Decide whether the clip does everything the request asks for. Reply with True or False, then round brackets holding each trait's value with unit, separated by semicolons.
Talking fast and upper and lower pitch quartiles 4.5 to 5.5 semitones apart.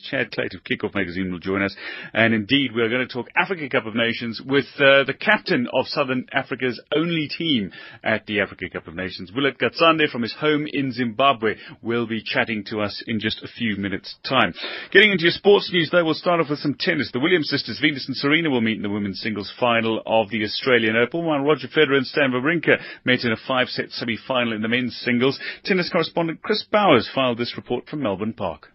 True (220 wpm; 5.0 semitones)